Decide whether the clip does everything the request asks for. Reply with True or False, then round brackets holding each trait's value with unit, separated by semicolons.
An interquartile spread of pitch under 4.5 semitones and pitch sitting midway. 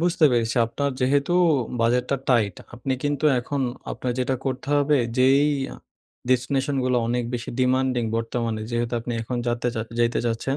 False (2.6 semitones; 125 Hz)